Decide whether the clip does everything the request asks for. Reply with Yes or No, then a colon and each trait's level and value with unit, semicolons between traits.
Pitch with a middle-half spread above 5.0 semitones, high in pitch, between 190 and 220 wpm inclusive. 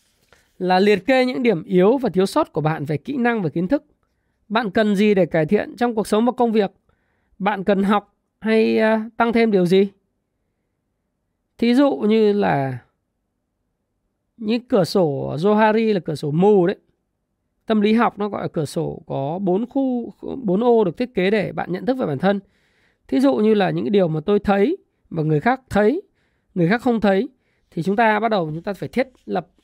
No: average, 4.3 semitones; high, 205 Hz; average, 200 wpm